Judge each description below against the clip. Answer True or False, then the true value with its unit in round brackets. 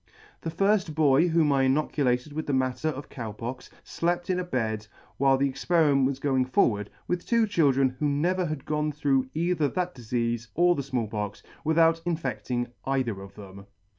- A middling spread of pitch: True (4.6 semitones)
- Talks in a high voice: False (140 Hz)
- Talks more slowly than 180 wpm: False (185 wpm)